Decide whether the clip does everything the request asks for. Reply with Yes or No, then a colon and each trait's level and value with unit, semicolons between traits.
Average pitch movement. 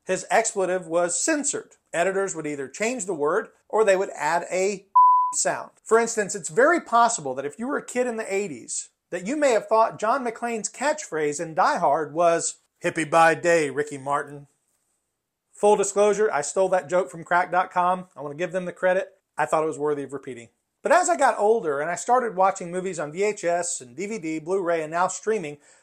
Yes: average, 4.9 semitones